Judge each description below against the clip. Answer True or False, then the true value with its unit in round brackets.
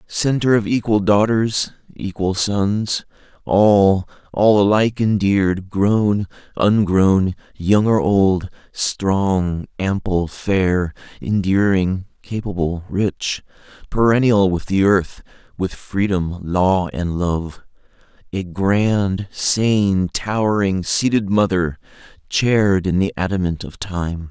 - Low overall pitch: True (100 Hz)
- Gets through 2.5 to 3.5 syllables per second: True (3.2 syllables/s)